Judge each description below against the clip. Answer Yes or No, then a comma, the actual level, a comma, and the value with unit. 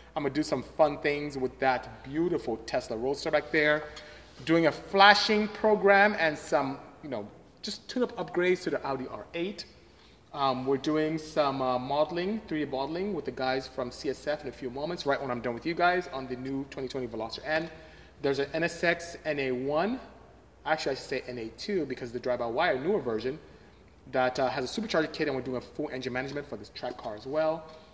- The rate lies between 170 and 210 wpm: Yes, average, 200 wpm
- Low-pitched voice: No, medium, 150 Hz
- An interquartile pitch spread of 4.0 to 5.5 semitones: Yes, average, 4.3 semitones